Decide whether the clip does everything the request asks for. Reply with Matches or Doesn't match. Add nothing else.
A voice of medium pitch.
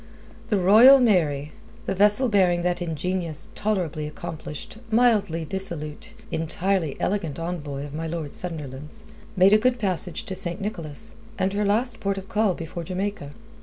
Matches